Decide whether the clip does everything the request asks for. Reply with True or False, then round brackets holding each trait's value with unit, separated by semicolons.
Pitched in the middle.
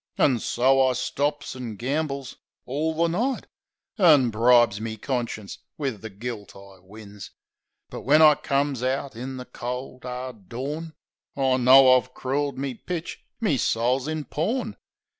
False (130 Hz)